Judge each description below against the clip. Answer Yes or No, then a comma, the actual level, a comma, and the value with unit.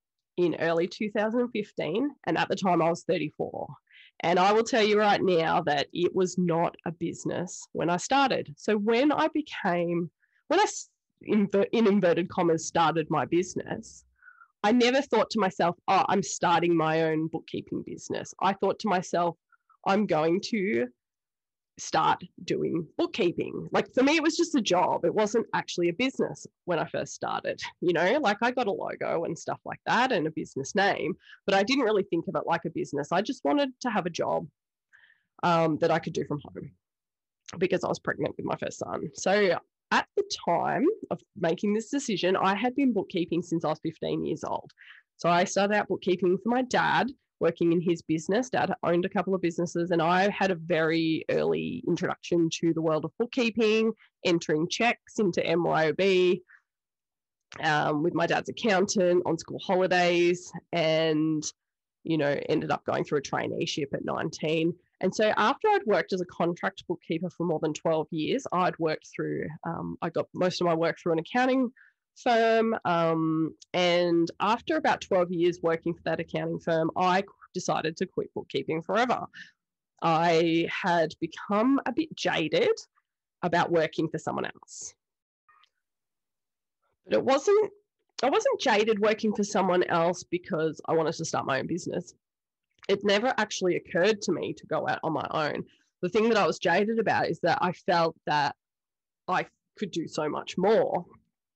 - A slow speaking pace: No, average, 175 wpm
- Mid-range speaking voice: Yes, medium, 180 Hz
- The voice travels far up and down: No, average, 4.8 semitones